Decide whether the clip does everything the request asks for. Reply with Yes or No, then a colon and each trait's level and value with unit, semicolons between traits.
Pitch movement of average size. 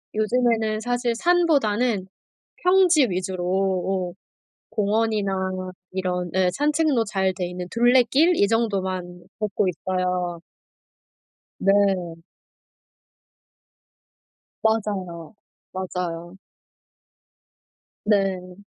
Yes: average, 4.1 semitones